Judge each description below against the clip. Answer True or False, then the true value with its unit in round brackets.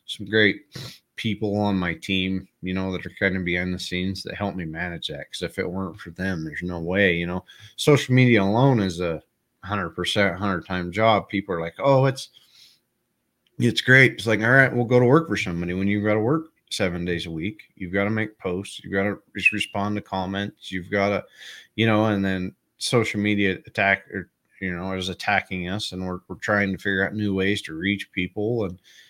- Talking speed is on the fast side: True (225 wpm)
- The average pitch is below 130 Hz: True (100 Hz)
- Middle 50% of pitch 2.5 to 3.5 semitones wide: True (2.9 semitones)